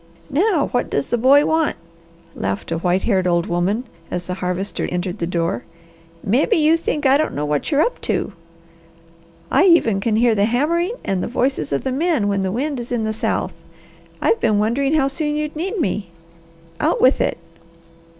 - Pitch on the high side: Yes, high, 235 Hz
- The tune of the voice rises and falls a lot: Yes, wide, 8.3 semitones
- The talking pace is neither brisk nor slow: Yes, average, 190 wpm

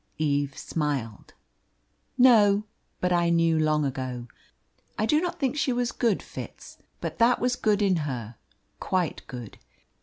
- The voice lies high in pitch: No, medium, 170 Hz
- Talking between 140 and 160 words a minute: Yes, average, 145 wpm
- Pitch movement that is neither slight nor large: No, wide, 8.5 semitones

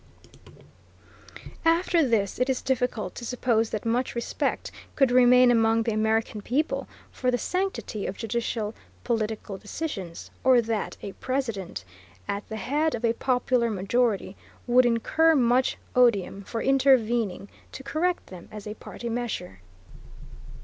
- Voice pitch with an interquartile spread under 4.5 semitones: Yes, average, 2.9 semitones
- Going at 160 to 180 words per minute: No, slow, 135 wpm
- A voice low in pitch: No, high, 235 Hz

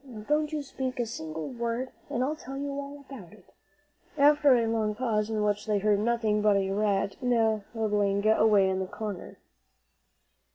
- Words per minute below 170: No, average, 175 wpm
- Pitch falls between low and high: No, high, 220 Hz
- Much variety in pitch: No, average, 3.8 semitones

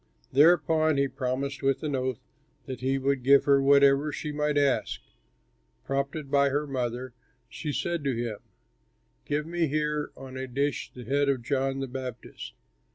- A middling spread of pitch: No, narrow, 2.0 semitones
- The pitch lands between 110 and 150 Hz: Yes, medium, 140 Hz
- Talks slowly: No, average, 160 wpm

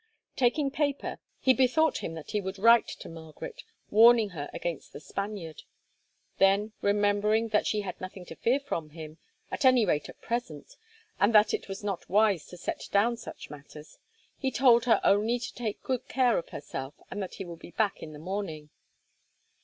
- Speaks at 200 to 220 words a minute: No, average, 185 wpm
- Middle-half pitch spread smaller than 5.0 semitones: No, wide, 5.6 semitones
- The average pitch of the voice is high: Yes, high, 205 Hz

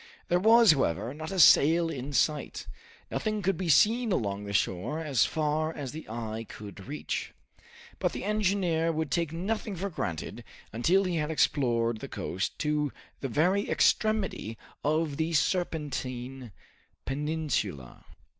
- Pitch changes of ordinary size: No, wide, 6.3 semitones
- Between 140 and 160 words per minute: Yes, average, 145 wpm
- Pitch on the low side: No, medium, 155 Hz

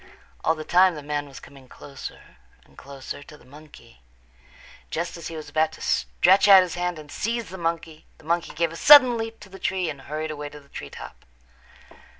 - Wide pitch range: No, average, 3.7 semitones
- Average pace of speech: No, fast, 210 wpm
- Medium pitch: Yes, medium, 160 Hz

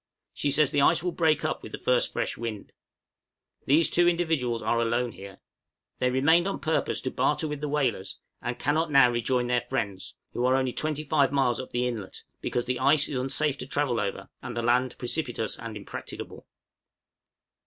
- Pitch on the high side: No, low, 130 Hz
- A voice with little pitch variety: No, average, 3.9 semitones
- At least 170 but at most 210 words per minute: Yes, average, 185 wpm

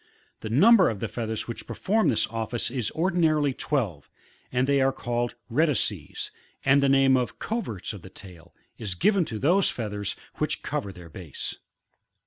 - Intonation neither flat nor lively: No, wide, 5.9 semitones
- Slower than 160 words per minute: No, average, 165 wpm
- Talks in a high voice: No, low, 120 Hz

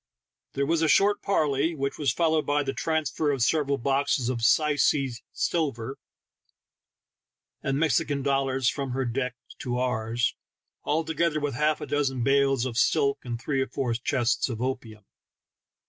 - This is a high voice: No, low, 135 Hz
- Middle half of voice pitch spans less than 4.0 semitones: Yes, average, 3.1 semitones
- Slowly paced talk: No, average, 155 wpm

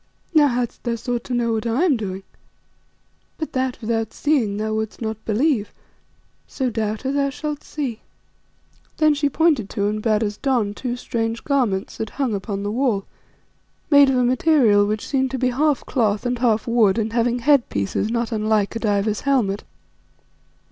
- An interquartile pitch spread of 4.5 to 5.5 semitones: No, average, 3.7 semitones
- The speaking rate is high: No, average, 175 wpm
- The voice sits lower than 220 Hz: No, high, 235 Hz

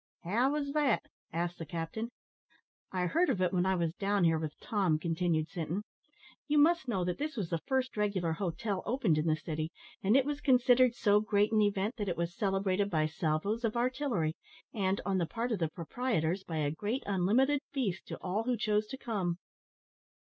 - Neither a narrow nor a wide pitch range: No, wide, 5.8 semitones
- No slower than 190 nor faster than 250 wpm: Yes, average, 200 wpm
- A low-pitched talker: No, high, 200 Hz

